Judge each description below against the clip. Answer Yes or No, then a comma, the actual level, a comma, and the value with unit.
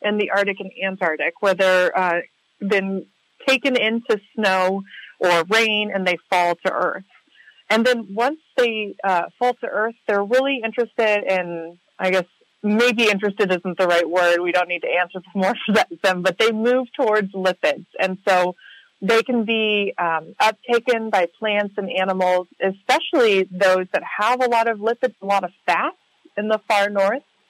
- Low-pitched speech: No, high, 200 Hz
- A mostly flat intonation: No, average, 3.4 semitones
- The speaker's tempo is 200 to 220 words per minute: No, average, 170 wpm